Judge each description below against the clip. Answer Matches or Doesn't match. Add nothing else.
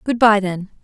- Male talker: Doesn't match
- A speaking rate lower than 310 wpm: Matches